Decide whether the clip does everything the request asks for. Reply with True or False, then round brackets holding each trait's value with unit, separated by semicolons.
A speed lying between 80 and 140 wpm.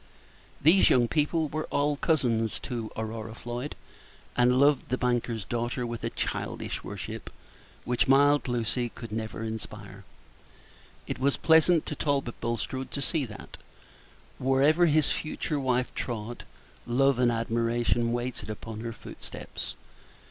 True (135 wpm)